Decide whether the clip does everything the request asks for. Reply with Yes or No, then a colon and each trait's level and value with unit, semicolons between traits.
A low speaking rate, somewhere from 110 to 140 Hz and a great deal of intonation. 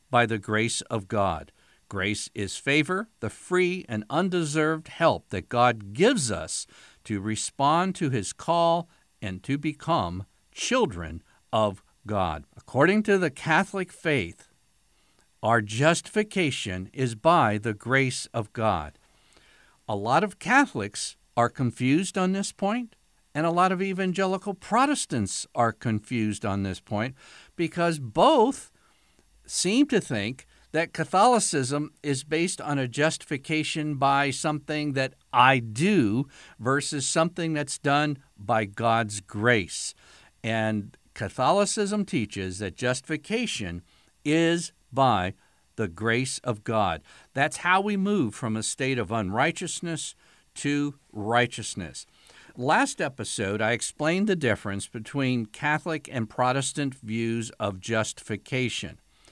Yes: slow, 120 wpm; low, 135 Hz; wide, 7.0 semitones